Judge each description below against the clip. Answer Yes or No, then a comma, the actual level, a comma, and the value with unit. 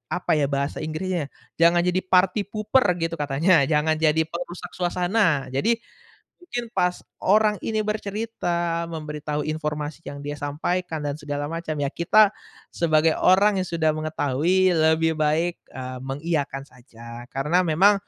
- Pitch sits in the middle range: Yes, medium, 165 Hz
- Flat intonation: No, average, 3.6 semitones